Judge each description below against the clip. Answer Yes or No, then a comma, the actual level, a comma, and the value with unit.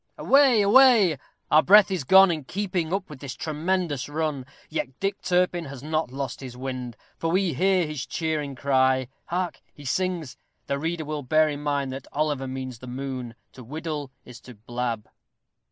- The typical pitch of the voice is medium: Yes, medium, 150 Hz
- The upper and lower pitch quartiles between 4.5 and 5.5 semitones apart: Yes, average, 5.1 semitones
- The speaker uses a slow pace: No, average, 175 wpm